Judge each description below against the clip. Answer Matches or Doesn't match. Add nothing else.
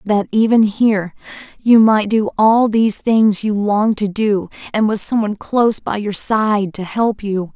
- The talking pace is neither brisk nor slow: Matches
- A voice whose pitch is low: Doesn't match